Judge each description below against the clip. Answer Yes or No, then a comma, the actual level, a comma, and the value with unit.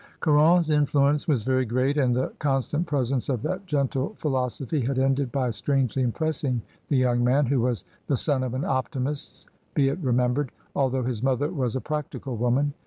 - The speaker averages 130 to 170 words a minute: No, average, 180 wpm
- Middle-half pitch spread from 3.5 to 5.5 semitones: No, narrow, 2.5 semitones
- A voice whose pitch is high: No, low, 135 Hz